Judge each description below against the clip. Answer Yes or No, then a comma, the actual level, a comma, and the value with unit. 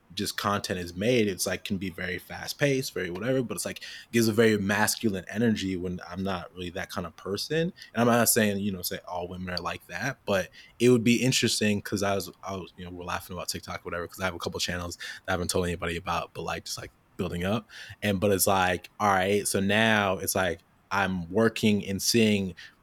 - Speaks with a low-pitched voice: Yes, low, 100 Hz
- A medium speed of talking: No, fast, 240 wpm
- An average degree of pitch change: Yes, average, 3.3 semitones